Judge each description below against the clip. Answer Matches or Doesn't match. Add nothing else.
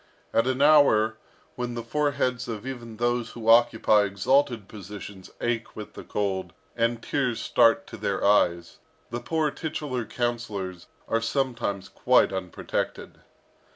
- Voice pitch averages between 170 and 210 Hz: Doesn't match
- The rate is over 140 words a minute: Doesn't match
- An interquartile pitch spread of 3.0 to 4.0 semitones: Matches